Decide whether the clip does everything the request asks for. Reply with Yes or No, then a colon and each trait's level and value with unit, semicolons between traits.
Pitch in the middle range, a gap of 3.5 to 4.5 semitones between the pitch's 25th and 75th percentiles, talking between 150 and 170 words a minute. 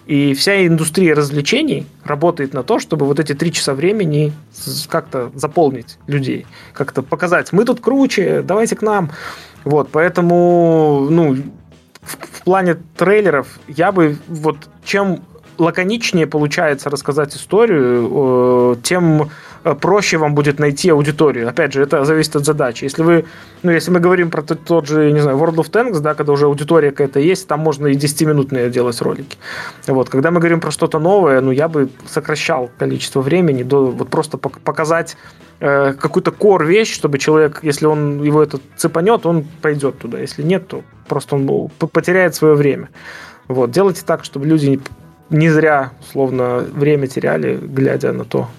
No: medium, 155 Hz; average, 3.0 semitones; fast, 160 wpm